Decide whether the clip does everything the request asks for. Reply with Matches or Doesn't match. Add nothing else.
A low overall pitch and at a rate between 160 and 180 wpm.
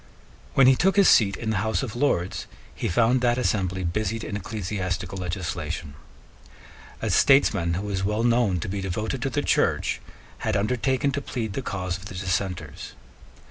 Matches